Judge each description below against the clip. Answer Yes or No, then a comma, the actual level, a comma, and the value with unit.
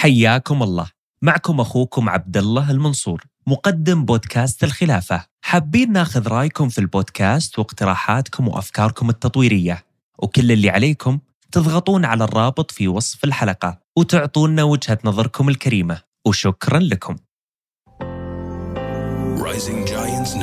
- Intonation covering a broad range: Yes, wide, 6.3 semitones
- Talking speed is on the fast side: No, average, 95 wpm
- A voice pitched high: No, low, 120 Hz